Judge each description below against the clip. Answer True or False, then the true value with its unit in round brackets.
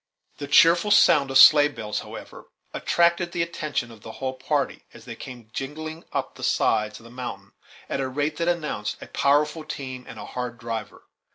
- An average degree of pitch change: True (4.3 semitones)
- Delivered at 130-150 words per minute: False (190 wpm)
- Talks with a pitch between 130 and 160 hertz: True (140 Hz)